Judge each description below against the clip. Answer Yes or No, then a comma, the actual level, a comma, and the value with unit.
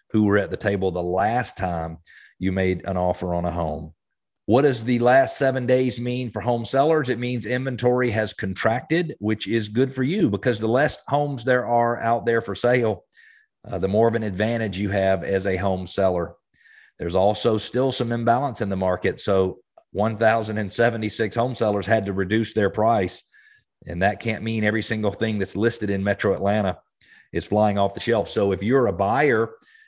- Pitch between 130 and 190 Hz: No, low, 110 Hz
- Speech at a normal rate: Yes, average, 195 wpm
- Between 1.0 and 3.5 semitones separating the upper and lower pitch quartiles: No, average, 3.9 semitones